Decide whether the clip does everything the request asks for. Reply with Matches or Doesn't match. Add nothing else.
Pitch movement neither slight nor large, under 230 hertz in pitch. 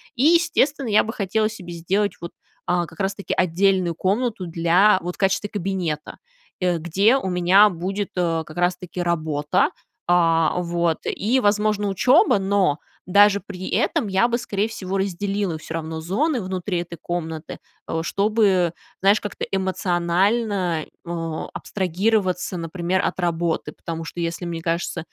Matches